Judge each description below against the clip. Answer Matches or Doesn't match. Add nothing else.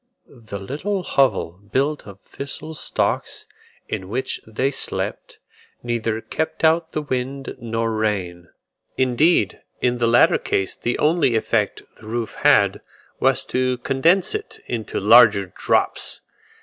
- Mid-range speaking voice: Doesn't match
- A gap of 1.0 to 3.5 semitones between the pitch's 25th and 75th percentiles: Doesn't match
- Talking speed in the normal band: Doesn't match